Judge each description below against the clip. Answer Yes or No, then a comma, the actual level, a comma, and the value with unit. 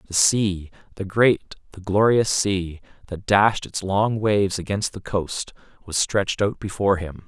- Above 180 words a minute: No, average, 150 wpm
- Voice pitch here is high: No, low, 100 Hz